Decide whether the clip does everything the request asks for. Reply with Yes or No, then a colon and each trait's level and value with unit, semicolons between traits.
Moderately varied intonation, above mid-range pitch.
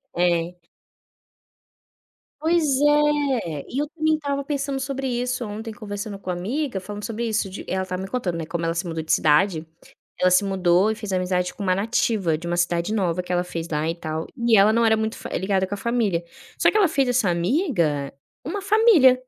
No: wide, 6.3 semitones; high, 205 Hz